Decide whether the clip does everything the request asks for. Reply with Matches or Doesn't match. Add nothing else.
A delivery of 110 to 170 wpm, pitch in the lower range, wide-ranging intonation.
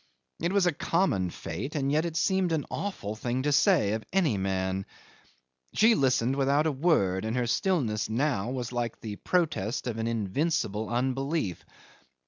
Matches